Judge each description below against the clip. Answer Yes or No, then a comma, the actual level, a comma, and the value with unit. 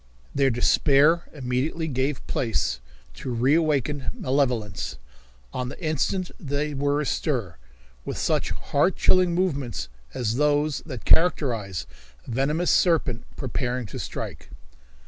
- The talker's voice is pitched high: No, medium, 140 Hz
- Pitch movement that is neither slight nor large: Yes, average, 3.8 semitones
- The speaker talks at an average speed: No, slow, 115 wpm